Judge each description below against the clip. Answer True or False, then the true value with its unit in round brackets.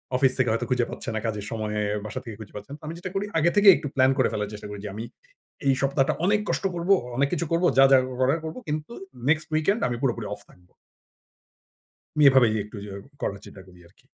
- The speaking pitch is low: True (130 Hz)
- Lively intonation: True (6.5 semitones)